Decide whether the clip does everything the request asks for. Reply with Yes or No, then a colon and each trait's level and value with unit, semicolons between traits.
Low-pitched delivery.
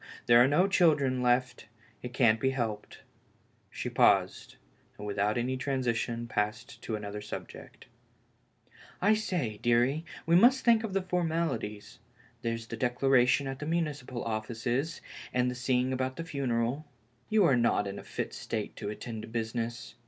Yes: low, 125 Hz